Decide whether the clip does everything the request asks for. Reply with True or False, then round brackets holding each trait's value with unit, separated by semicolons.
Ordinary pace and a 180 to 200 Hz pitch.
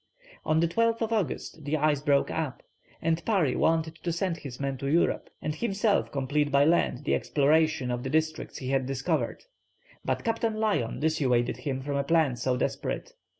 False (180 wpm; 155 Hz)